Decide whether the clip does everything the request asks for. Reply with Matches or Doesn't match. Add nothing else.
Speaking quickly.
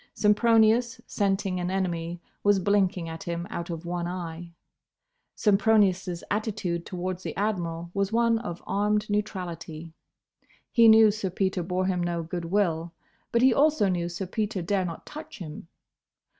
Doesn't match